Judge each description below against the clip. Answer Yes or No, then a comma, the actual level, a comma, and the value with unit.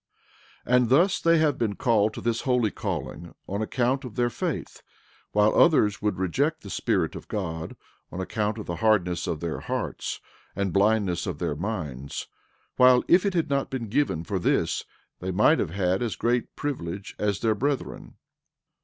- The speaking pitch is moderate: No, low, 105 Hz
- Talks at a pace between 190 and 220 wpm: No, average, 175 wpm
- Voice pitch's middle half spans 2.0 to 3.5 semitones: No, average, 5.3 semitones